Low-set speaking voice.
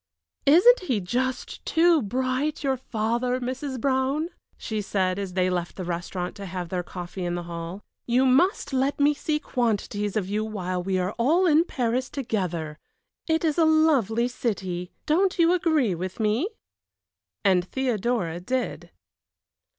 No: high, 235 Hz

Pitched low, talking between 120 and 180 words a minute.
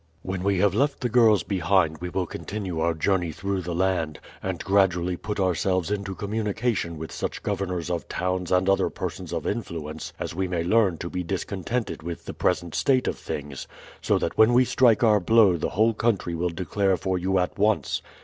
No: very low, 95 Hz; average, 195 wpm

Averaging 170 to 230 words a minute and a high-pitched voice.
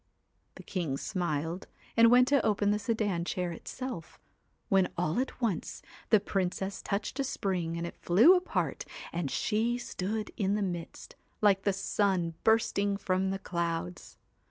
No: average, 150 wpm; high, 195 Hz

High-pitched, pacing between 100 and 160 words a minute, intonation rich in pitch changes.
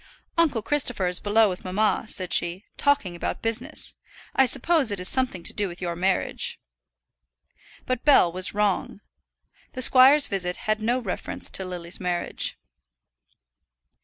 Yes: high, 210 Hz; average, 145 wpm; wide, 5.8 semitones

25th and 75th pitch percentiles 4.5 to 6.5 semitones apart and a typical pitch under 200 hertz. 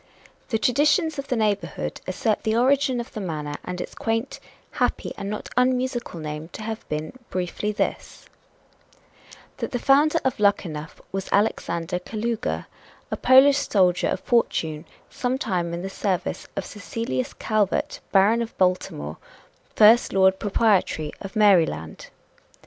No: average, 4.9 semitones; high, 205 Hz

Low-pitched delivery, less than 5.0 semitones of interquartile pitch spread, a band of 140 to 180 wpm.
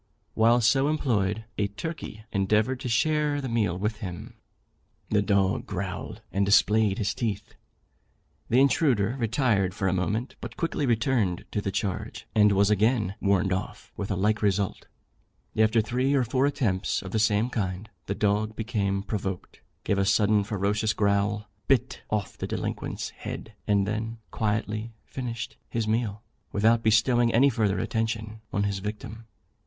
Yes: low, 110 Hz; narrow, 2.6 semitones; average, 155 wpm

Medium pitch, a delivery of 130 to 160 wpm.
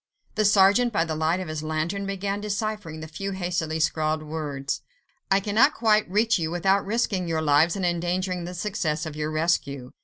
No: medium, 175 Hz; average, 185 wpm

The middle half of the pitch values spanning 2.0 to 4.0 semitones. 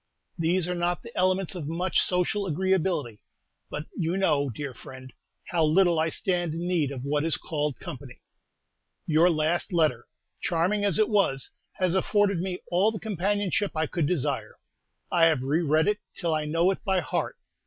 Yes: average, 3.7 semitones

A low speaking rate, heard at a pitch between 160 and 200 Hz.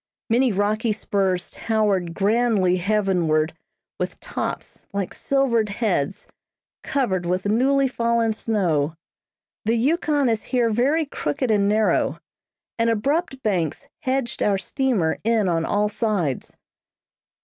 No: slow, 115 wpm; high, 215 Hz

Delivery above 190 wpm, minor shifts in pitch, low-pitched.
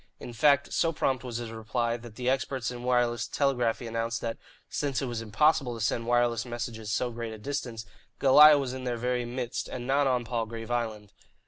Yes: average, 200 wpm; narrow, 2.1 semitones; low, 120 Hz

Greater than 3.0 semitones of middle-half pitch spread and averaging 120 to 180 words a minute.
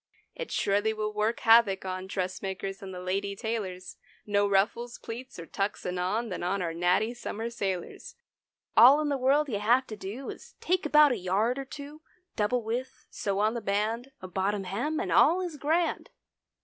No: average, 4.5 semitones; average, 190 wpm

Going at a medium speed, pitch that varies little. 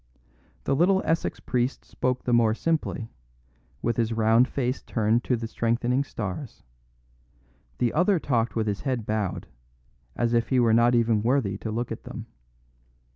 Yes: average, 160 wpm; narrow, 2.3 semitones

